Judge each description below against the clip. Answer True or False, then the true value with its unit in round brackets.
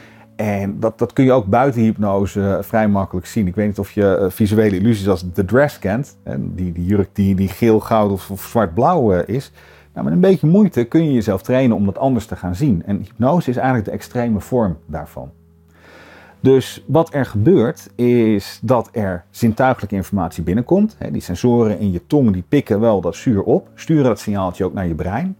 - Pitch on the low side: True (105 Hz)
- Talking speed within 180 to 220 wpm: True (200 wpm)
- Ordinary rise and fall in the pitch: True (4.1 semitones)